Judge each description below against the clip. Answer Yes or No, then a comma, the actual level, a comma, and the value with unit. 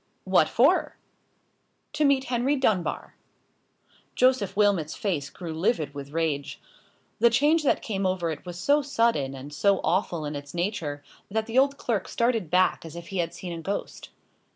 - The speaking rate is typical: Yes, average, 170 wpm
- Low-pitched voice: No, medium, 185 Hz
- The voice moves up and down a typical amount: No, wide, 6.5 semitones